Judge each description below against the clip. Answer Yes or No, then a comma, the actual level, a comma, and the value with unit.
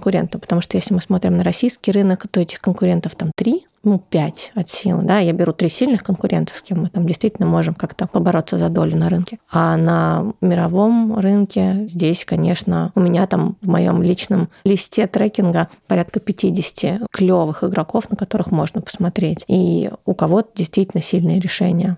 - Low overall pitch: No, medium, 185 Hz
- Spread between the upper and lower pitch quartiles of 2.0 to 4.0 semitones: Yes, narrow, 2.5 semitones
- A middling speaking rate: No, fast, 170 wpm